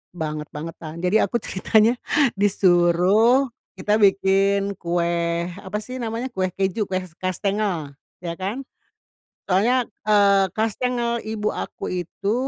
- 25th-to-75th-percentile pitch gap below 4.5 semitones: Yes, average, 3.6 semitones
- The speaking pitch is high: Yes, high, 195 Hz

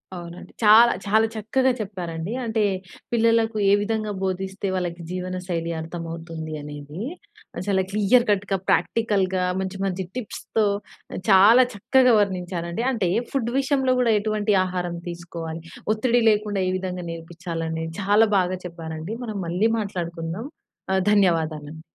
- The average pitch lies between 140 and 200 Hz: Yes, high, 190 Hz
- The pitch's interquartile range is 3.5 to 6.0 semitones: Yes, average, 4.0 semitones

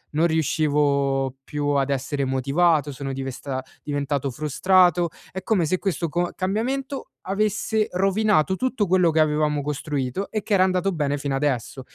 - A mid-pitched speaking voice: Yes, medium, 155 Hz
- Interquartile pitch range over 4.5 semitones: Yes, average, 5.1 semitones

